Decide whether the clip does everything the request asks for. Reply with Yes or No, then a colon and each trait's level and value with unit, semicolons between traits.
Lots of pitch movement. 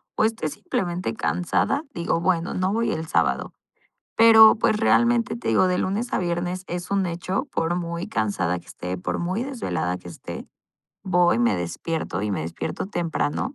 Yes: wide, 8.8 semitones